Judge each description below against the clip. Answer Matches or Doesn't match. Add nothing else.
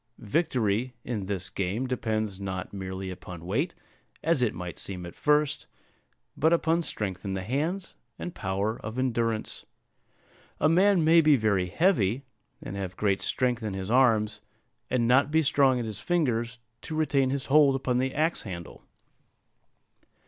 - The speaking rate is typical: Matches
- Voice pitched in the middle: Doesn't match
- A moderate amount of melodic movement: Doesn't match